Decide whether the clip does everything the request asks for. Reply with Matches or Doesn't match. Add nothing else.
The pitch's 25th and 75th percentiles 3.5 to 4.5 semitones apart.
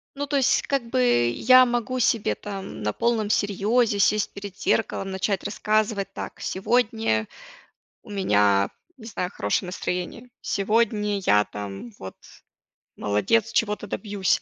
Matches